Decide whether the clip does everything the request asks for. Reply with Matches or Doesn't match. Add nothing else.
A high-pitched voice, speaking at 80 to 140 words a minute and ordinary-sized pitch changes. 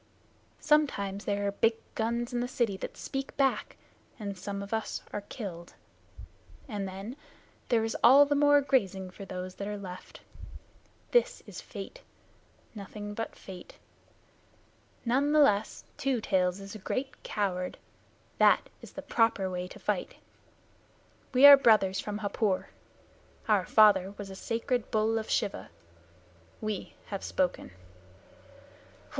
Matches